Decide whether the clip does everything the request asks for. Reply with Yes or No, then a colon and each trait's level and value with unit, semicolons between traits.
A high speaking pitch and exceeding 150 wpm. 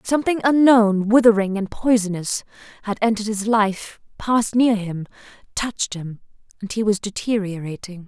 No: high, 210 Hz; slow, 135 wpm